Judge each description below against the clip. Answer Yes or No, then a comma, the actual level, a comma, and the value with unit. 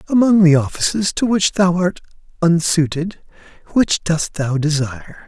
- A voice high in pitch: No, medium, 170 Hz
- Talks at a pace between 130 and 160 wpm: Yes, slow, 135 wpm